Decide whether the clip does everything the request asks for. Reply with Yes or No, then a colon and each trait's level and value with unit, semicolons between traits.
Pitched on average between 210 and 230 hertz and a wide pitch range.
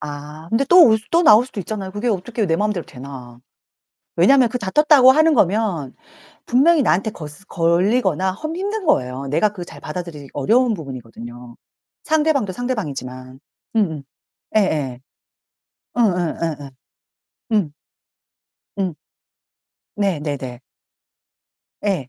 No: high, 190 Hz; wide, 8.0 semitones